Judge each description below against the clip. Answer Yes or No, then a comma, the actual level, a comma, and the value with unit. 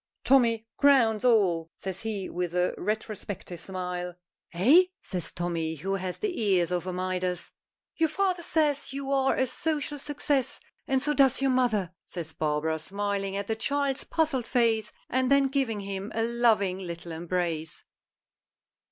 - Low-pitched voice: No, high, 210 Hz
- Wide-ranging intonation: Yes, wide, 6.9 semitones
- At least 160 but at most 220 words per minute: No, average, 150 wpm